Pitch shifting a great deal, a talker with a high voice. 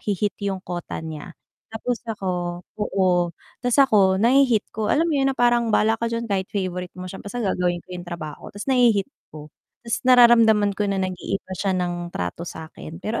No: average, 4.4 semitones; high, 200 Hz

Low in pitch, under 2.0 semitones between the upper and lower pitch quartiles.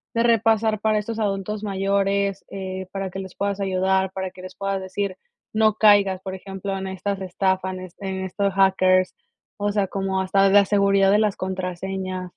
No: high, 195 Hz; narrow, 1.2 semitones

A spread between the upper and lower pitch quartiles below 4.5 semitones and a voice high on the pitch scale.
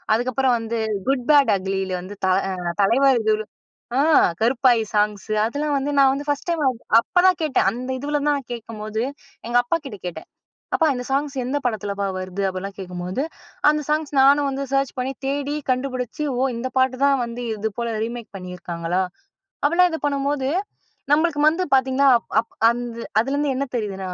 No: average, 4.8 semitones; very high, 255 Hz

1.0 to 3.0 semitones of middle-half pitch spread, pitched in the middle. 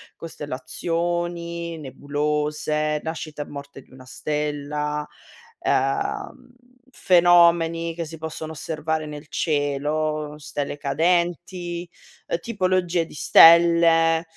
Yes: narrow, 2.4 semitones; medium, 160 Hz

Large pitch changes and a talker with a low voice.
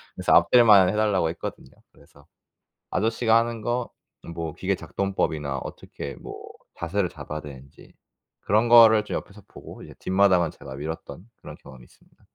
Yes: wide, 6.0 semitones; very low, 95 Hz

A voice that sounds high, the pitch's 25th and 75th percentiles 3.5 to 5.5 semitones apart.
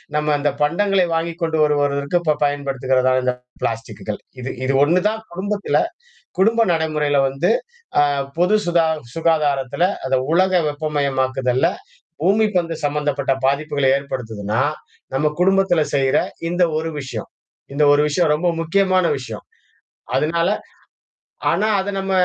No: medium, 150 Hz; average, 4.4 semitones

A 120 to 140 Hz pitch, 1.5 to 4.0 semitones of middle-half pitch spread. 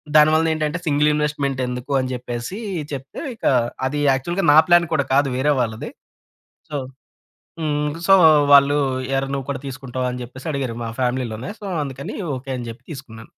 Yes: low, 135 Hz; average, 2.9 semitones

